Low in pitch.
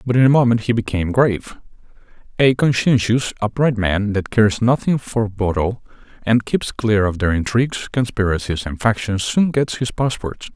Yes: low, 110 Hz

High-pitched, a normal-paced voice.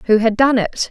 No: high, 235 Hz; fast, 265 wpm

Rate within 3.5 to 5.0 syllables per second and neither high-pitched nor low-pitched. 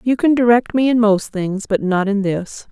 No: 4.7 syllables/s; high, 215 Hz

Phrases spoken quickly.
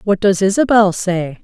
No: average, 165 wpm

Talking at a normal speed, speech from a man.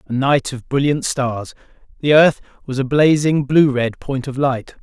Yes: average, 185 wpm; male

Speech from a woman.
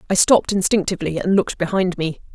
Yes: female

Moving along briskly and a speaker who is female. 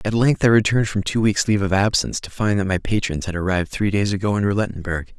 No: fast, 255 wpm; male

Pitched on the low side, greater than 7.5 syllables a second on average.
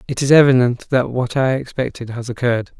No: low, 125 Hz; 5.8 syllables/s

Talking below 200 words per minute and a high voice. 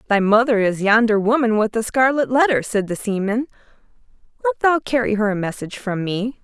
Yes: average, 185 wpm; high, 225 Hz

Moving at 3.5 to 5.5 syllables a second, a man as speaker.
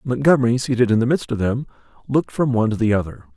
No: 7.3 syllables/s; male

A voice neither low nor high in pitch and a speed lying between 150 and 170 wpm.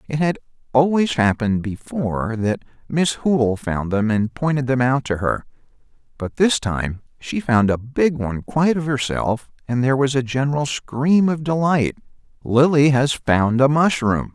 No: low, 130 Hz; average, 165 wpm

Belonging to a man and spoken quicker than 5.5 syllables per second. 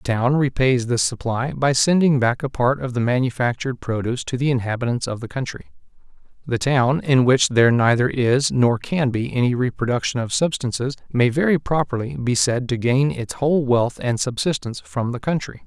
No: male; 5.3 syllables/s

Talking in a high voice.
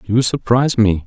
No: low, 115 Hz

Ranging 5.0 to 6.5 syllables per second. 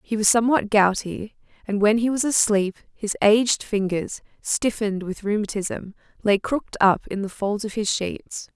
No: 4.8 syllables/s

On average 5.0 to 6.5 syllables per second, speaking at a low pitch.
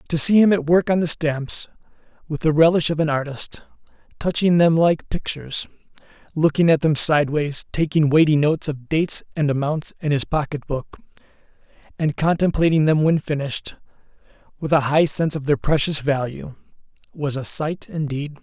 No: 5.3 syllables/s; medium, 155 Hz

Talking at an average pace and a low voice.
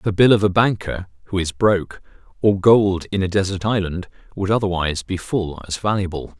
Yes: average, 190 wpm; very low, 95 Hz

